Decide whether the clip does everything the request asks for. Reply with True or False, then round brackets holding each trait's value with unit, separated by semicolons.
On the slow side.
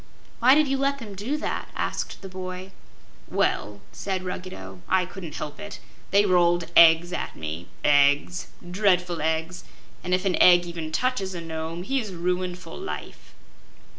False (165 wpm)